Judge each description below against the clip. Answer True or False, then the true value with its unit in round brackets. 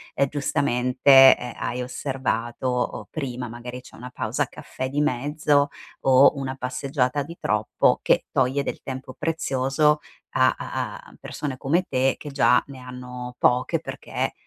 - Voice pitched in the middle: False (130 Hz)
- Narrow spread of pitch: True (2.1 semitones)